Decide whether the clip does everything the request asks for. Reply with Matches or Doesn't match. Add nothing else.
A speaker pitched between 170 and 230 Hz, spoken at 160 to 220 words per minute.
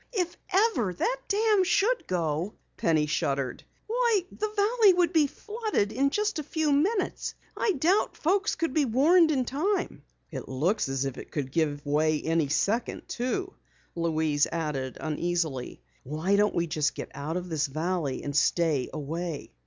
Matches